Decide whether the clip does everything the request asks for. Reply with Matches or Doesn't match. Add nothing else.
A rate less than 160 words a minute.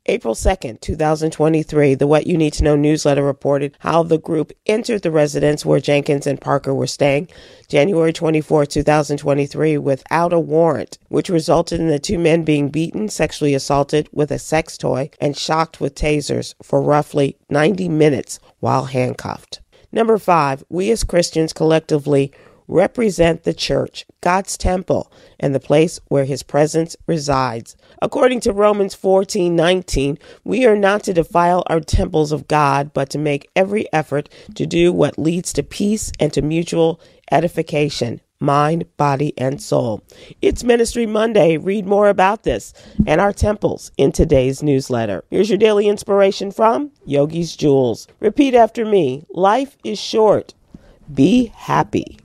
Matches